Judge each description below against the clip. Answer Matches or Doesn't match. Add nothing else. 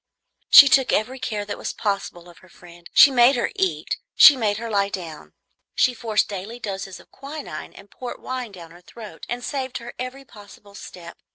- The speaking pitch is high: Matches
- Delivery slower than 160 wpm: Doesn't match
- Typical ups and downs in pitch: Matches